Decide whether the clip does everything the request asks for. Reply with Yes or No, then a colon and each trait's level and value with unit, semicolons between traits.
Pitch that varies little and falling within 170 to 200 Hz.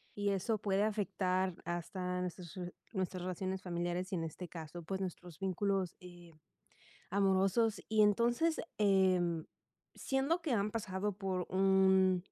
Yes: narrow, 2.1 semitones; high, 190 Hz